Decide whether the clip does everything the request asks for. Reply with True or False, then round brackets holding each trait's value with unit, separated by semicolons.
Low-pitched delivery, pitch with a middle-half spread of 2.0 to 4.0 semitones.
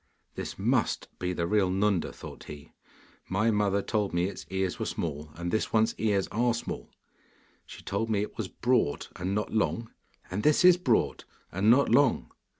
True (105 Hz; 3.7 semitones)